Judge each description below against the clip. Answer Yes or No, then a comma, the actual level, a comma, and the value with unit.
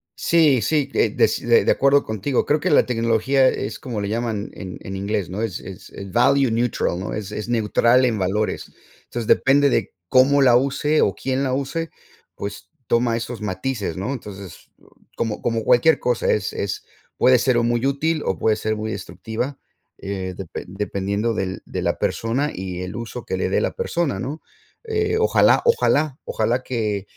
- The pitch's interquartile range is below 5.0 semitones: Yes, average, 4.6 semitones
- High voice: No, low, 115 Hz